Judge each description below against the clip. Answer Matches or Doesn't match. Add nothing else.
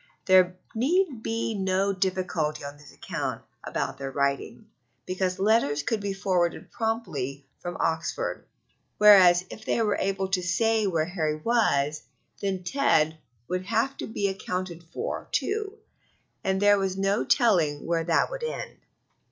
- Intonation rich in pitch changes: Doesn't match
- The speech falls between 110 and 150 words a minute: Matches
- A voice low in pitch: Doesn't match